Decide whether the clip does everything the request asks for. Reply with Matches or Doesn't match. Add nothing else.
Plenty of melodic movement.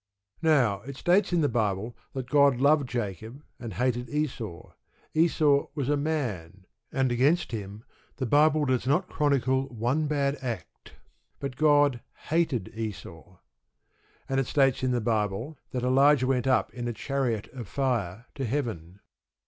Doesn't match